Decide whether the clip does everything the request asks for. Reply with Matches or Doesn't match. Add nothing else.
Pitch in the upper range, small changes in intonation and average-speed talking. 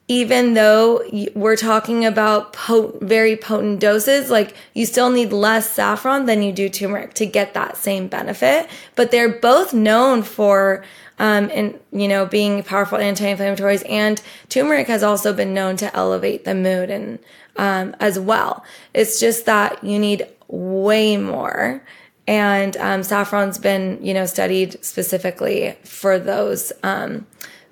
Matches